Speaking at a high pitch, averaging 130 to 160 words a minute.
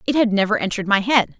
No: high, 215 Hz; fast, 260 wpm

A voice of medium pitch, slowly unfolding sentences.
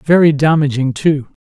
Yes: medium, 145 Hz; slow, 125 wpm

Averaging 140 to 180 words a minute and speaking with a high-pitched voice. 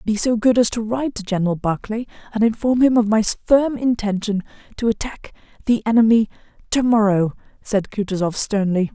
Yes: average, 160 wpm; high, 220 Hz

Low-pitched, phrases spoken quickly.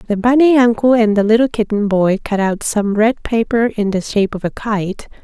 No: high, 215 Hz; fast, 220 wpm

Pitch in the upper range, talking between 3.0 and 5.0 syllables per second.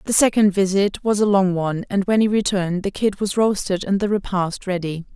No: high, 195 Hz; 5.5 syllables/s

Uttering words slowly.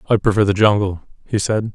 No: fast, 205 wpm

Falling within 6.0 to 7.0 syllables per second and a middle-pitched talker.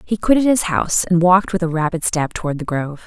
Yes: 6.5 syllables/s; medium, 175 Hz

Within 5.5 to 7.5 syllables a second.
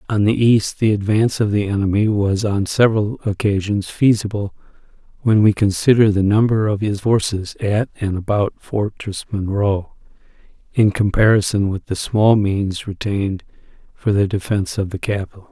No: 4.9 syllables/s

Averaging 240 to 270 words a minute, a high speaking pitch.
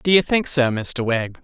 No: fast, 250 wpm; medium, 140 Hz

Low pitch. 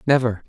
Yes: low, 115 Hz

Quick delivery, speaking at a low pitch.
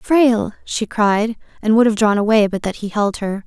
No: fast, 225 wpm; high, 215 Hz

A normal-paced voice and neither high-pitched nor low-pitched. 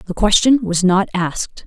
No: average, 180 wpm; high, 195 Hz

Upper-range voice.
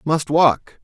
No: medium, 155 Hz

